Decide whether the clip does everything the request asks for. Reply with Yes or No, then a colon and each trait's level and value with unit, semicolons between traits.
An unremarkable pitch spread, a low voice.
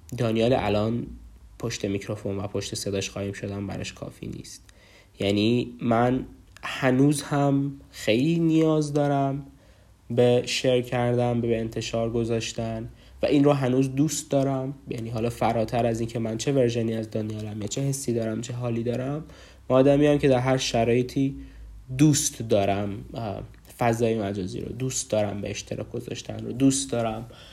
Yes: average, 3.8 semitones; low, 115 Hz